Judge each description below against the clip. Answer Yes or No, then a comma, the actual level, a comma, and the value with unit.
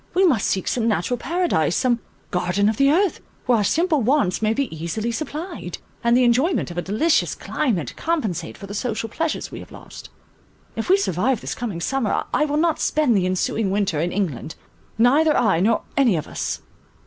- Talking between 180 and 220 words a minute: Yes, average, 195 wpm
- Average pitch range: No, wide, 7.6 semitones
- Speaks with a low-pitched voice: No, high, 230 Hz